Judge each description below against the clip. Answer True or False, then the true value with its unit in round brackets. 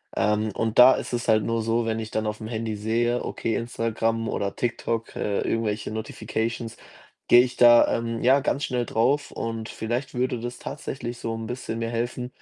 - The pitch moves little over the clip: True (1.5 semitones)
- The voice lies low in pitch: True (115 Hz)